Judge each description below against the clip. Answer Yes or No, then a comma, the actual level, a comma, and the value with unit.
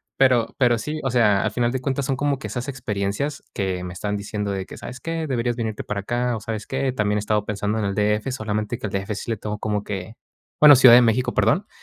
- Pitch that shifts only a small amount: No, average, 3.6 semitones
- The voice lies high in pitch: No, low, 110 Hz